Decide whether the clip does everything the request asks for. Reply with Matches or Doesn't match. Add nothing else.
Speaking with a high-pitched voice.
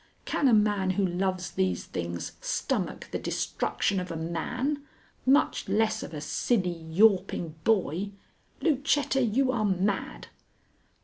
Matches